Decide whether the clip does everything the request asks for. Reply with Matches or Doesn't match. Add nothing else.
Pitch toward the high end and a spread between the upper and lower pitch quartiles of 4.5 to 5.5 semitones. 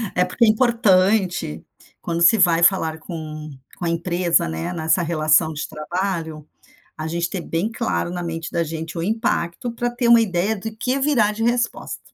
Doesn't match